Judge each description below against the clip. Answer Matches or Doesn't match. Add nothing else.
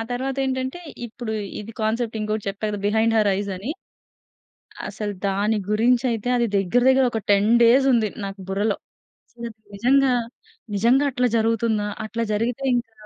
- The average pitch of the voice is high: Matches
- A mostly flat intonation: Doesn't match